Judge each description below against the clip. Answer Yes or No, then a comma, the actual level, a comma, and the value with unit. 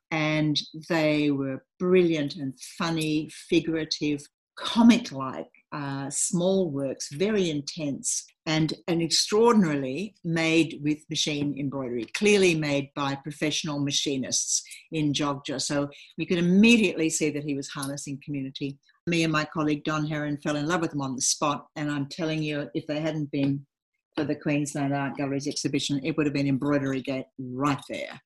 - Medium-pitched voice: Yes, medium, 150 Hz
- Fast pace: No, average, 155 wpm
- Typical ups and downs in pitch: No, narrow, 2.3 semitones